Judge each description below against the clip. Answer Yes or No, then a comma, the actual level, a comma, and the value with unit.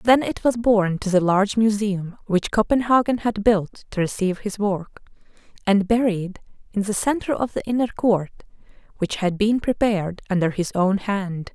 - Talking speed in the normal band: Yes, average, 170 wpm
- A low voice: No, high, 205 Hz